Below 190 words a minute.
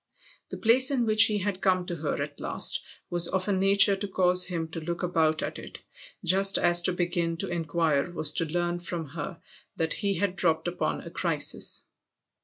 No: average, 200 wpm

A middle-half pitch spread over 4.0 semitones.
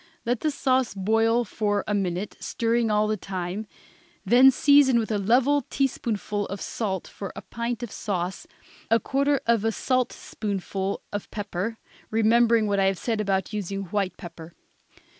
No: average, 3.2 semitones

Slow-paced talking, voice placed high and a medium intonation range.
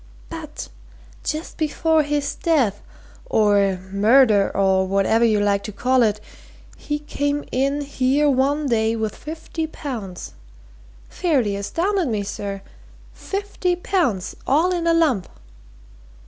No: slow, 120 wpm; very high, 265 Hz; wide, 7.0 semitones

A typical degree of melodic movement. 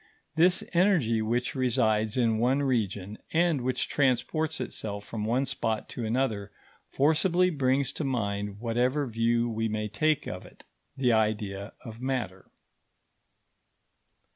Yes: average, 4.0 semitones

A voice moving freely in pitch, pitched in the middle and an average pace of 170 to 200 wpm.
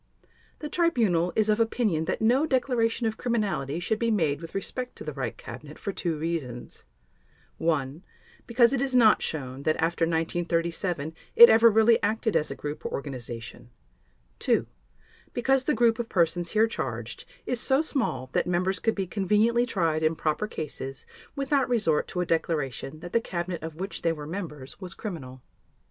Yes: wide, 6.4 semitones; medium, 180 Hz; average, 175 wpm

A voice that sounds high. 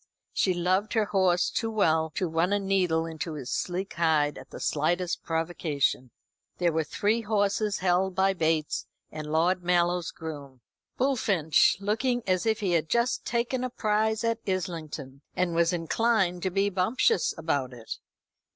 No: medium, 180 Hz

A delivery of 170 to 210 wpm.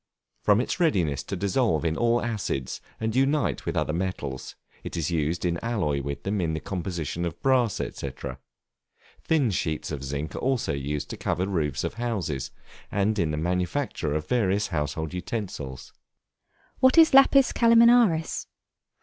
No: average, 160 wpm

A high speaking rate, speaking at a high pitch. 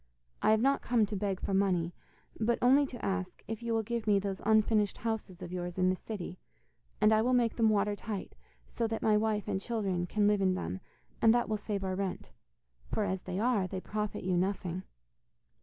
Yes: fast, 210 wpm; high, 205 Hz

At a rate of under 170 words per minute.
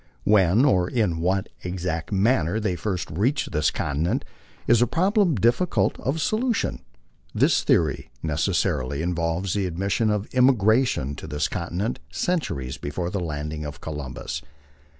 Yes: average, 145 wpm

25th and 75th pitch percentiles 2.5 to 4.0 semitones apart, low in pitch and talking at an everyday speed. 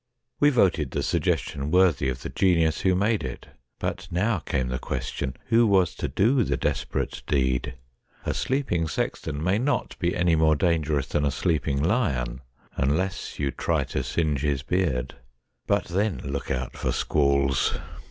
No: average, 5.2 semitones; very low, 80 Hz; average, 160 wpm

